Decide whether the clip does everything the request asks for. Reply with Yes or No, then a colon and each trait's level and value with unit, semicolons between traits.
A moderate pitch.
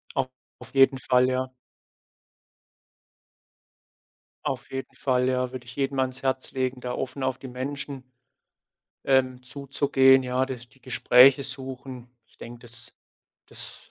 No: low, 130 Hz